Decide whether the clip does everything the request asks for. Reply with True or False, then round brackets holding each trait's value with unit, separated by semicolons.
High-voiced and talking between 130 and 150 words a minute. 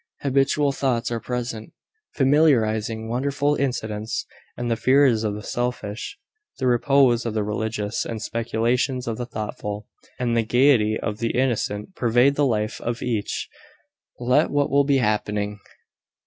False (120 Hz; 145 wpm)